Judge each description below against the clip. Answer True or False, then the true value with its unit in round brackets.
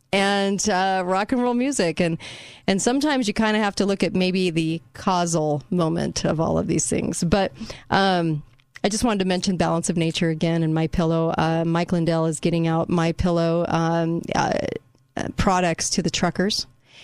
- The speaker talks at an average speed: True (185 wpm)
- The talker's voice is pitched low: False (175 Hz)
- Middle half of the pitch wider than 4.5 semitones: False (3.0 semitones)